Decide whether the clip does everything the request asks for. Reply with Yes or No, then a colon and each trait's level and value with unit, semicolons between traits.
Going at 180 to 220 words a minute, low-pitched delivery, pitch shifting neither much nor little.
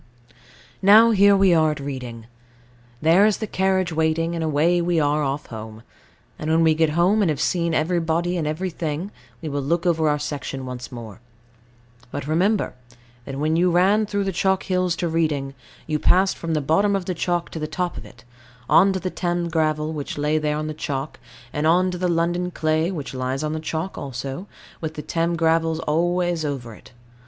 No: average, 200 wpm; medium, 160 Hz; average, 3.0 semitones